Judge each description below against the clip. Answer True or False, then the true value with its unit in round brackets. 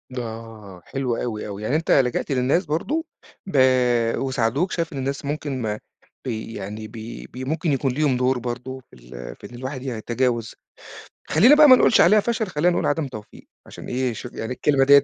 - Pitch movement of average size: True (4.5 semitones)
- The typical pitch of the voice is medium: False (130 Hz)